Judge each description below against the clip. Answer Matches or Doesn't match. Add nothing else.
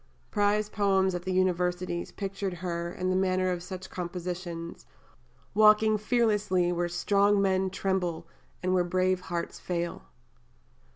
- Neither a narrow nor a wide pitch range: Doesn't match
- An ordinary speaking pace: Doesn't match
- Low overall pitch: Doesn't match